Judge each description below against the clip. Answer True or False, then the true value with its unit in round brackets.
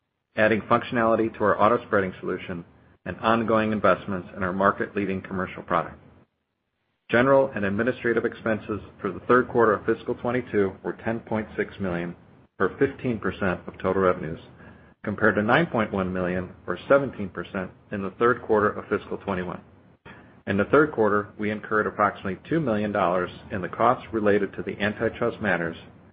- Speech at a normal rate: True (170 wpm)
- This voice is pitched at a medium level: False (105 Hz)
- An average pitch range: True (3.4 semitones)